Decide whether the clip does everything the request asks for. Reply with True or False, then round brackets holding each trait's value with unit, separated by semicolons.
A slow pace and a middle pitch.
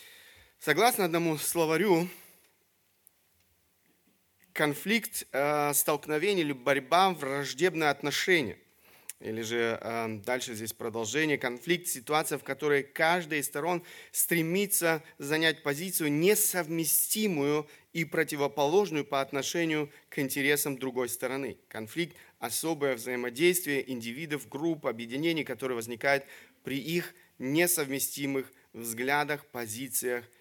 True (90 wpm; 145 Hz)